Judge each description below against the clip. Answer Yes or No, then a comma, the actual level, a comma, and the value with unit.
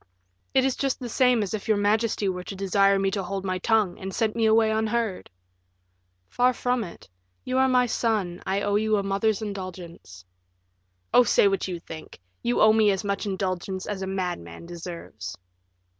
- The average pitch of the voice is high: Yes, high, 200 Hz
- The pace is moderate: Yes, average, 190 wpm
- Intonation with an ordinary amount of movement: Yes, average, 3.1 semitones